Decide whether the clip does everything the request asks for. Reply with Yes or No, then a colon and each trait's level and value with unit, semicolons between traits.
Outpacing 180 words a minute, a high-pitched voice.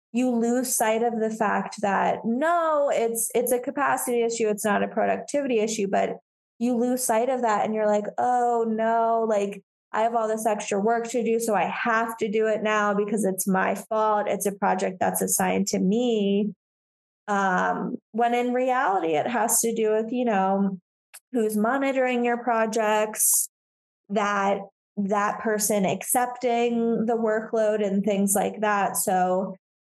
No: average, 165 wpm; high, 225 Hz